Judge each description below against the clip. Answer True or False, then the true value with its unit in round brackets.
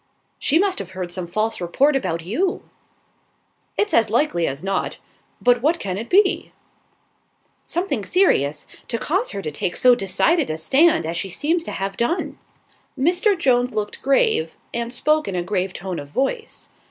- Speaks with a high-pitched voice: True (235 Hz)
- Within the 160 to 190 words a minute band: True (170 wpm)